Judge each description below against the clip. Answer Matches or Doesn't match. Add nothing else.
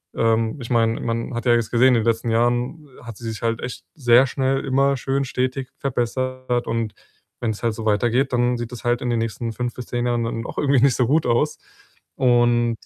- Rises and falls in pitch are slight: Matches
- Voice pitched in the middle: Doesn't match